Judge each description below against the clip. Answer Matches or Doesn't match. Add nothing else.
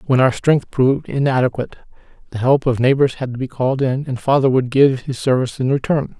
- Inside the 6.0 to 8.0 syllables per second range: Matches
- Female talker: Doesn't match